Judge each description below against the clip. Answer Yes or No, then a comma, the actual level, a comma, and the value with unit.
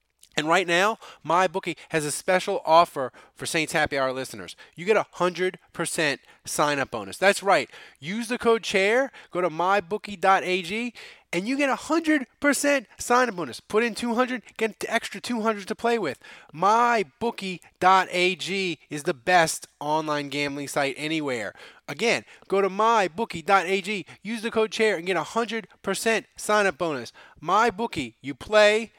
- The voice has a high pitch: Yes, high, 195 Hz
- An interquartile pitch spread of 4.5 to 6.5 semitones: Yes, average, 5.1 semitones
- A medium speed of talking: Yes, average, 150 wpm